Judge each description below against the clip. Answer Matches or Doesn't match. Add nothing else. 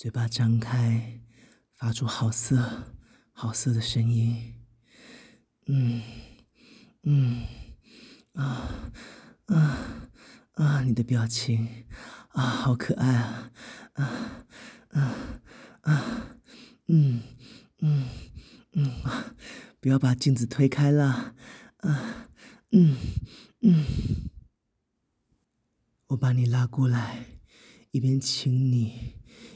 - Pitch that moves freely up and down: Doesn't match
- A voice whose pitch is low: Matches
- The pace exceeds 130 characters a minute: Doesn't match